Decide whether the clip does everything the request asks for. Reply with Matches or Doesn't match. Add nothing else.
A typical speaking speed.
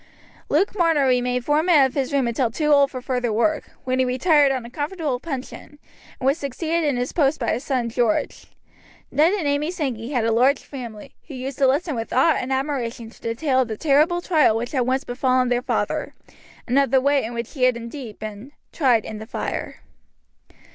Doesn't match